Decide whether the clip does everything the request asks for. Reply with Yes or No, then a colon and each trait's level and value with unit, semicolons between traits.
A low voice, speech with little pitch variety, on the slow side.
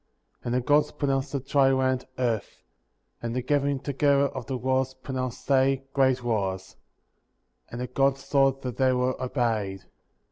No: low, 130 Hz; narrow, 1.6 semitones; average, 155 wpm